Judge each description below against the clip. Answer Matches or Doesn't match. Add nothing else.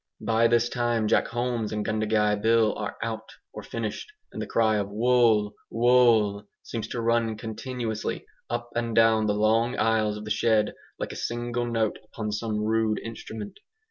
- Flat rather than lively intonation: Matches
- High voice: Doesn't match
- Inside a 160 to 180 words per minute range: Matches